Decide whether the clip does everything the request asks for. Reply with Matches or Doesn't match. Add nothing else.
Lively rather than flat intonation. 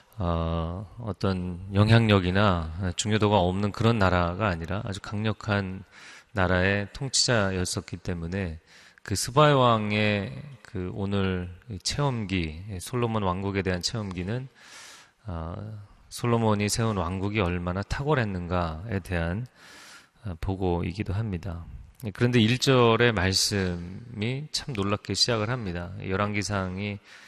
Doesn't match